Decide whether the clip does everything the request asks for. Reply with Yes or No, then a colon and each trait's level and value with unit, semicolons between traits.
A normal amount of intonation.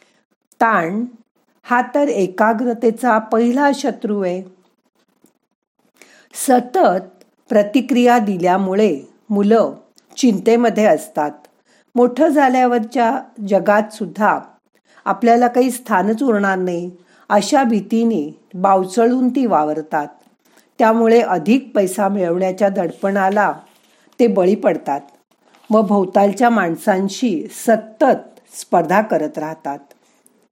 Yes: average, 4.1 semitones